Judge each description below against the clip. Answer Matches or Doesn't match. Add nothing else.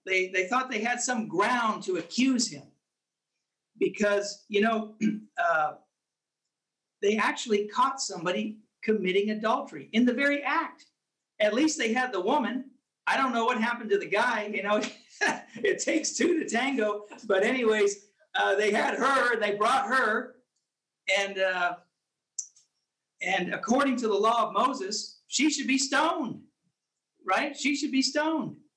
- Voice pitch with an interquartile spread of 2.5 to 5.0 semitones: Matches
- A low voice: Doesn't match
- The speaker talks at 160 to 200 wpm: Doesn't match